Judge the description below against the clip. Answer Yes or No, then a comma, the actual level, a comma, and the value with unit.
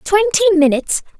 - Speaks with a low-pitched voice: No, very high, 375 Hz